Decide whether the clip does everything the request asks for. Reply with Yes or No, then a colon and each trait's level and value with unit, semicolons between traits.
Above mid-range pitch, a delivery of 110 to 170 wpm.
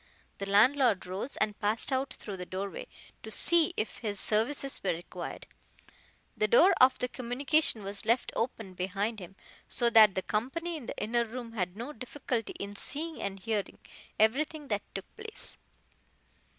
Yes: high, 225 Hz; average, 160 wpm